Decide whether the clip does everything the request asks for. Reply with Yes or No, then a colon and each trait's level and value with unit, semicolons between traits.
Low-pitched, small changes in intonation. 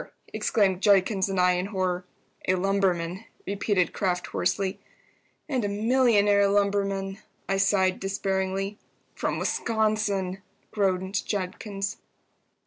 No: high, 195 Hz; narrow, 1.4 semitones